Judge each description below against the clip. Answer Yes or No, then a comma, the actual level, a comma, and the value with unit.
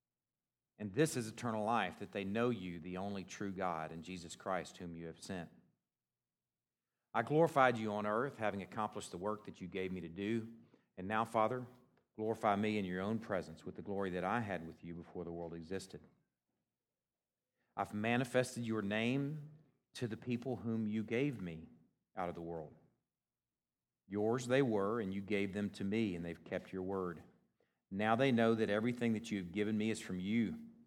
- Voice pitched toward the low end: Yes, low, 105 Hz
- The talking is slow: No, average, 190 wpm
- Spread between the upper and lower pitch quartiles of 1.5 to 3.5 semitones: No, average, 4.0 semitones